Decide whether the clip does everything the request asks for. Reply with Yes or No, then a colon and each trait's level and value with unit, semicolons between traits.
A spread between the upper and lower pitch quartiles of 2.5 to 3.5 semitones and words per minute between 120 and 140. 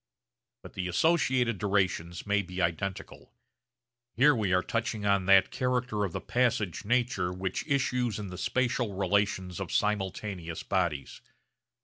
No: average, 4.6 semitones; slow, 135 wpm